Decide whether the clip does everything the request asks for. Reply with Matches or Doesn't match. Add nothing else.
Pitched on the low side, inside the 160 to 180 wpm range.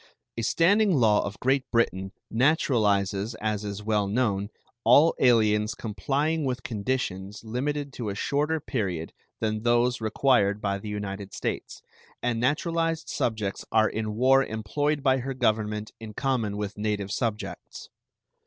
Doesn't match